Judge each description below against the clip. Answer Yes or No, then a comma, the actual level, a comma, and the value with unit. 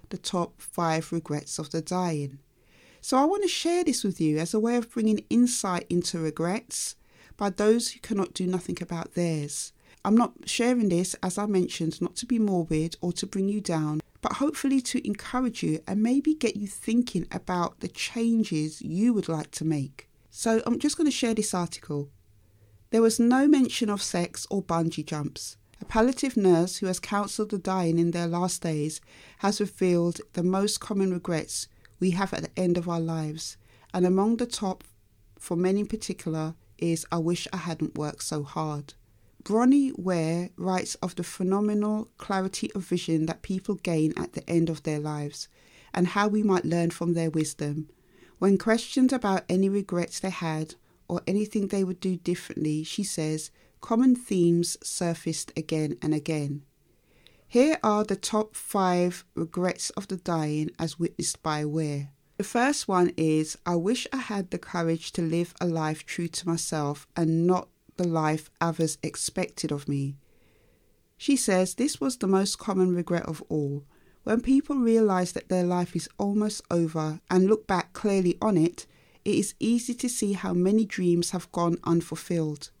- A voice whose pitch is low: No, medium, 175 Hz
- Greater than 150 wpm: Yes, average, 180 wpm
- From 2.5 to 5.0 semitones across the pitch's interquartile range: Yes, average, 4.6 semitones